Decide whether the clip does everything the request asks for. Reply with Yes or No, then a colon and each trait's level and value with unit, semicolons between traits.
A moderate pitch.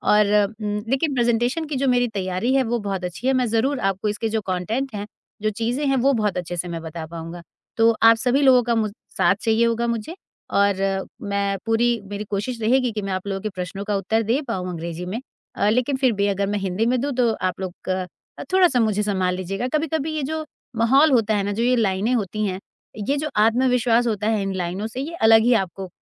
No: high, 220 Hz